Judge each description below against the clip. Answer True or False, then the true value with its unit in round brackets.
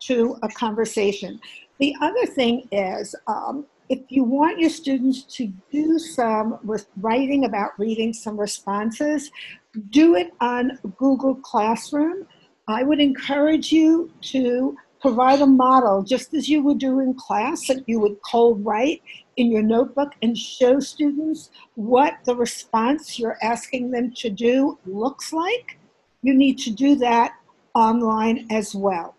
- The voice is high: True (255 Hz)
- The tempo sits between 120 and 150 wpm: True (145 wpm)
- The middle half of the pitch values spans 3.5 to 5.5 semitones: True (4.0 semitones)